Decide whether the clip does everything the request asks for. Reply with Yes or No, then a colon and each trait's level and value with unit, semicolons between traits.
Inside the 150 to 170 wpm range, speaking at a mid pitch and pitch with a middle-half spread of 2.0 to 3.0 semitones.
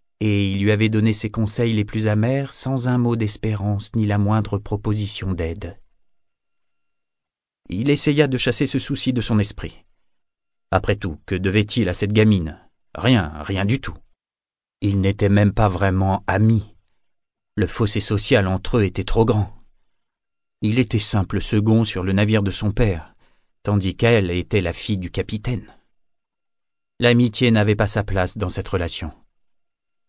No: average, 155 wpm; low, 105 Hz; average, 2.7 semitones